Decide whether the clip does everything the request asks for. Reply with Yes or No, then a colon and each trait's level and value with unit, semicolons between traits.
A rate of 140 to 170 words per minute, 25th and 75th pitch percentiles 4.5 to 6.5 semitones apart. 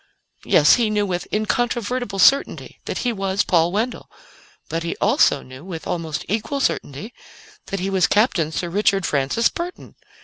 Yes: average, 160 wpm; average, 5.1 semitones